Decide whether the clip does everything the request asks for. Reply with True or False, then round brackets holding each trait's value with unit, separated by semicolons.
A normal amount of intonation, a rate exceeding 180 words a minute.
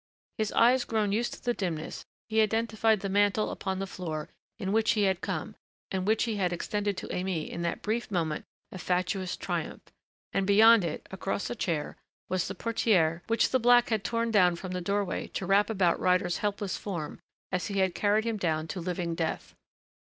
True (3.4 semitones; 195 wpm)